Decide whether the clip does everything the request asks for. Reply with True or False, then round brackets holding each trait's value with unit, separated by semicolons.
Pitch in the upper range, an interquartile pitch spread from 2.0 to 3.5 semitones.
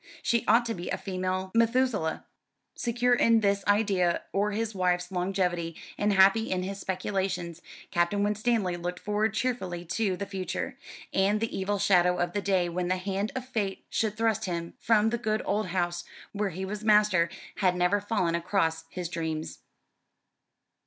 True (195 Hz; 3.1 semitones)